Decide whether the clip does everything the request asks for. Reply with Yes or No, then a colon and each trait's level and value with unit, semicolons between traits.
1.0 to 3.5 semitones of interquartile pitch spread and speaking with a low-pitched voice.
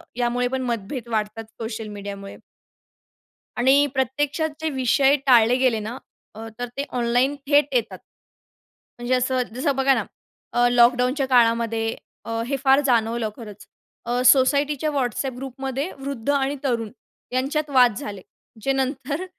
No: average, 2.8 semitones; very high, 250 Hz